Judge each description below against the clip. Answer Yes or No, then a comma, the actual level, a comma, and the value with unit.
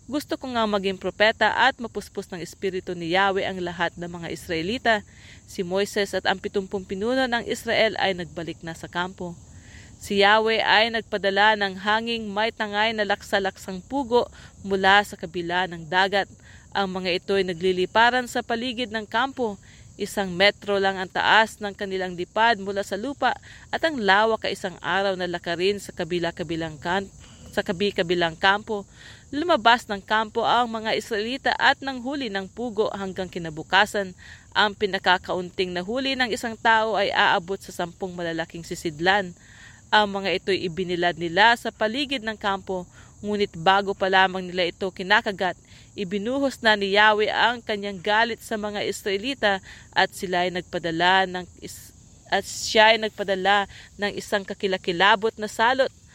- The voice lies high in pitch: Yes, high, 200 Hz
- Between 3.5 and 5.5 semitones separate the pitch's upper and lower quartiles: No, average, 3.1 semitones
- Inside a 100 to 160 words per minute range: Yes, average, 155 wpm